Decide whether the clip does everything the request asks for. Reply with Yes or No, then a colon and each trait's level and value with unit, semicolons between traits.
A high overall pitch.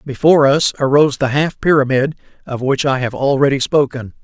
No: medium, 140 Hz